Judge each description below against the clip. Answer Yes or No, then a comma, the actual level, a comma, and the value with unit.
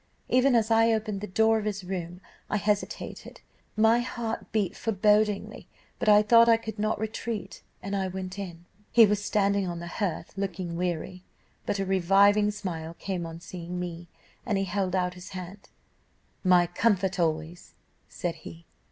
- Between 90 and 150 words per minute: No, average, 170 wpm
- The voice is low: No, high, 195 Hz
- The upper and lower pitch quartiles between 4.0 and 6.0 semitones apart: No, average, 3.0 semitones